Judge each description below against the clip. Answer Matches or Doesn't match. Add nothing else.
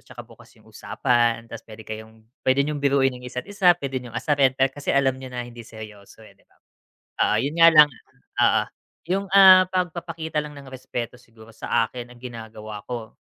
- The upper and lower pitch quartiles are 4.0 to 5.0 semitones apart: Matches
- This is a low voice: Matches